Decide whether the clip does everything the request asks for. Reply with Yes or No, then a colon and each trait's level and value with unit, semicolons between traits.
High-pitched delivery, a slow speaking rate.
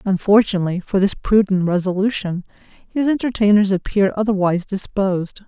Yes: high, 200 Hz; slow, 110 wpm